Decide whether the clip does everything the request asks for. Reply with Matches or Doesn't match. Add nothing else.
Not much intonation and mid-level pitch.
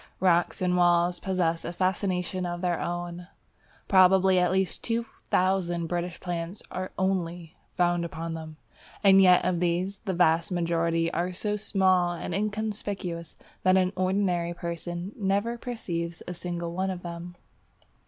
Matches